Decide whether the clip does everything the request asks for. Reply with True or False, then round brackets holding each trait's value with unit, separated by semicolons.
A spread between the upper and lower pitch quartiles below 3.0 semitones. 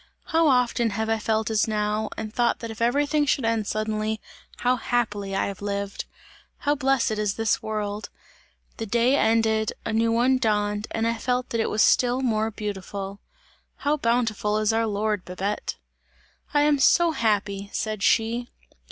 True (2.4 semitones)